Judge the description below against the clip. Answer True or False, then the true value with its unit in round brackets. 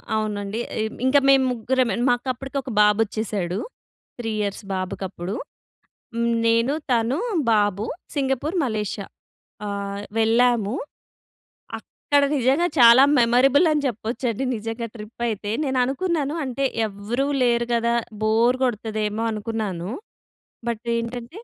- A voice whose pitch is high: True (230 Hz)